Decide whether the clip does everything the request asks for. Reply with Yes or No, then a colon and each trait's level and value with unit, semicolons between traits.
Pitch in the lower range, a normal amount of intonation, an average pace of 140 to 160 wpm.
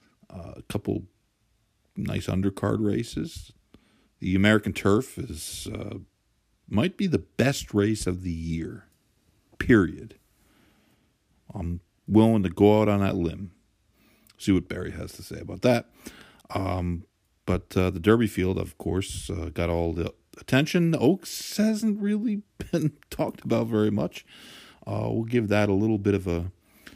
Yes: low, 100 Hz; average, 3.1 semitones; average, 145 wpm